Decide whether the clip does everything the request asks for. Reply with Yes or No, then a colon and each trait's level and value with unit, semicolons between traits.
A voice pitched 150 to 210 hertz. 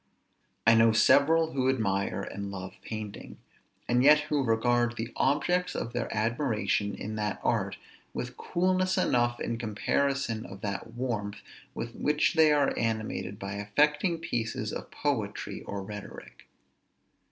No: low, 120 Hz